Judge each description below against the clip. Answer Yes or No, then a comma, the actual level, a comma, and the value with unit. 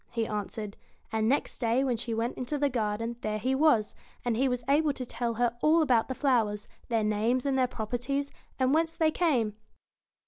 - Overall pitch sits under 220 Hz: No, high, 245 Hz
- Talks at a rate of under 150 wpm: No, average, 200 wpm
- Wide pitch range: No, average, 3.7 semitones